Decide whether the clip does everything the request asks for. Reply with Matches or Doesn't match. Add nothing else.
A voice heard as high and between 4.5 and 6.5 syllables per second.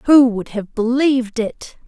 Doesn't match